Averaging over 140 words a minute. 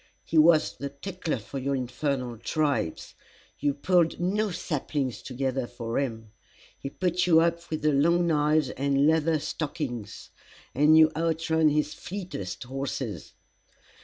No: slow, 135 wpm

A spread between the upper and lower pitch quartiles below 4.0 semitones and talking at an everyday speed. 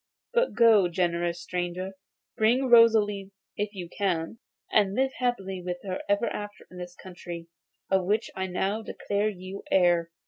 Yes: average, 3.1 semitones; average, 160 wpm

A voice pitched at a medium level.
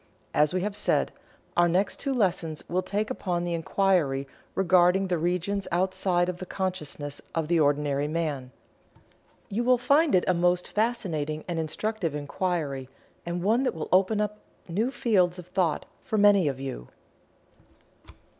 Yes: medium, 180 Hz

